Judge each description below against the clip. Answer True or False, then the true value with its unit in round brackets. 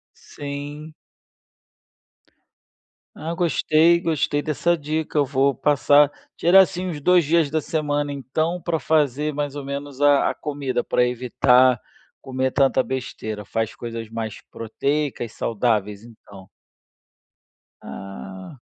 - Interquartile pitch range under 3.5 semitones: False (4.0 semitones)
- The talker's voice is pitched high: False (140 Hz)